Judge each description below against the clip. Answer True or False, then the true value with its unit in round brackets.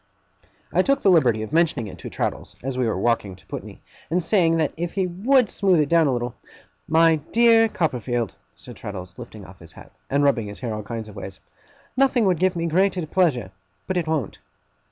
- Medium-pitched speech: True (155 Hz)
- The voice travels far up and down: True (7.9 semitones)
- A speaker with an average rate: False (210 wpm)